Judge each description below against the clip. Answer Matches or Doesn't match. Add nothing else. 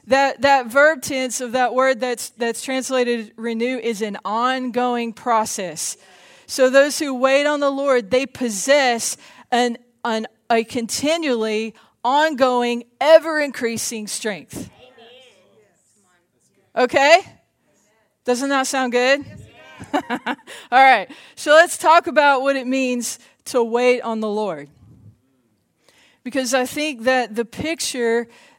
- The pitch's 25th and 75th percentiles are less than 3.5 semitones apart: Matches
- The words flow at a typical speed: Doesn't match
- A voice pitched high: Matches